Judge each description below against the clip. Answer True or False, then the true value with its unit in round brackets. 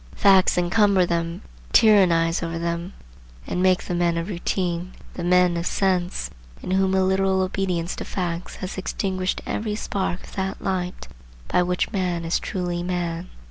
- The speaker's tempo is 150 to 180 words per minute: True (160 wpm)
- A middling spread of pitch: False (1.7 semitones)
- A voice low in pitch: False (180 Hz)